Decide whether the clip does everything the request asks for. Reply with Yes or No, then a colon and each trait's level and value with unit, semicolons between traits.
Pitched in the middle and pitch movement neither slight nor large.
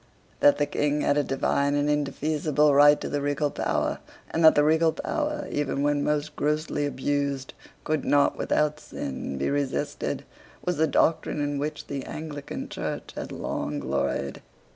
No: medium, 145 Hz; narrow, 1.1 semitones